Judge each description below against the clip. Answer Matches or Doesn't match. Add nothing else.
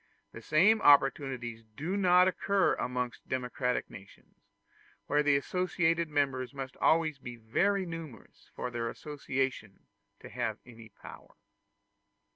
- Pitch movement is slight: Doesn't match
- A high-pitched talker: Doesn't match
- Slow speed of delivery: Matches